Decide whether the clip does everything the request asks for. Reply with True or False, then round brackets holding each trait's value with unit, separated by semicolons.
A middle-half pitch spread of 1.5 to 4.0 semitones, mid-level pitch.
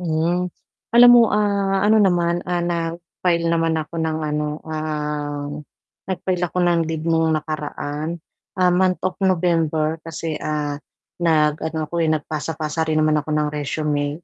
True (2.4 semitones; 160 Hz)